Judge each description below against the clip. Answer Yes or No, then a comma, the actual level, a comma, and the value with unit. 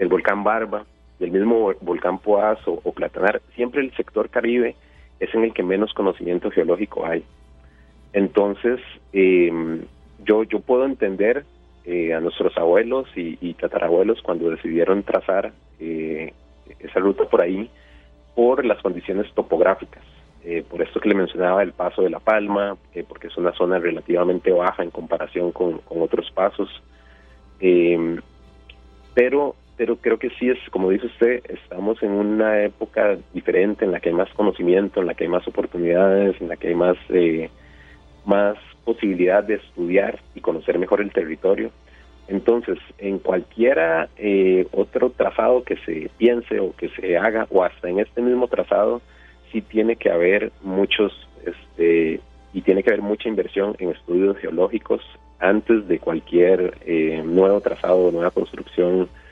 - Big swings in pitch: Yes, wide, 6.1 semitones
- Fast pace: No, average, 155 wpm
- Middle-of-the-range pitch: No, very low, 90 Hz